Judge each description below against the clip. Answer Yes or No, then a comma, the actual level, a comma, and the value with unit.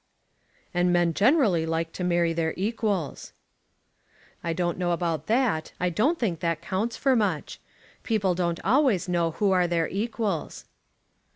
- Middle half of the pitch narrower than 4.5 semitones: Yes, average, 4.1 semitones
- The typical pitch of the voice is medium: Yes, medium, 180 Hz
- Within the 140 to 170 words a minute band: Yes, average, 150 wpm